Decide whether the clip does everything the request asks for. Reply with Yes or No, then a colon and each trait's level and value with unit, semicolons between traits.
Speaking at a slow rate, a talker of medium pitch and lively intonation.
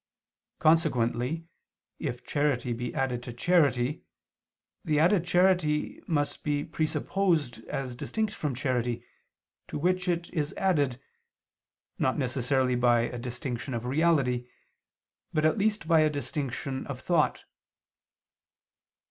No: slow, 115 wpm; medium, 145 Hz; average, 4.9 semitones